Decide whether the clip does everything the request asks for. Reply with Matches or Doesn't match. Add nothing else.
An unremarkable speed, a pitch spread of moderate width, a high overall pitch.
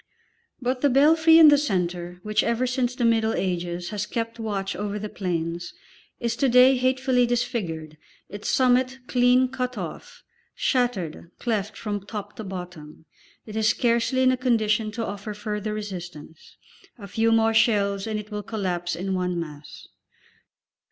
Matches